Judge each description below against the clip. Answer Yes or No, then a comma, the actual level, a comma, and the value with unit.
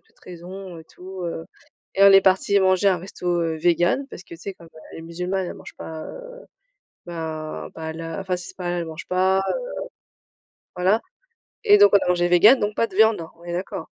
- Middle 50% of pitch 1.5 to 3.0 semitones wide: Yes, narrow, 2.4 semitones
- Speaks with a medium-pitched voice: Yes, medium, 180 Hz